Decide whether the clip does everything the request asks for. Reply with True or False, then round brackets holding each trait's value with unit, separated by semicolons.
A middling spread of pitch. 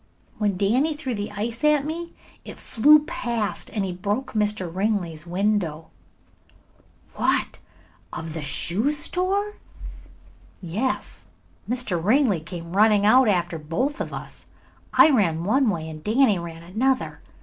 False (7.1 semitones)